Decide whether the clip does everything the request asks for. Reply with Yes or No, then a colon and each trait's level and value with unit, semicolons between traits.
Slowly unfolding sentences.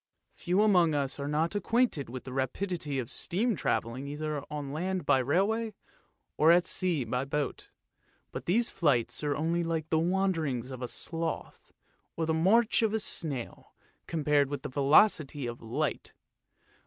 No: average, 160 wpm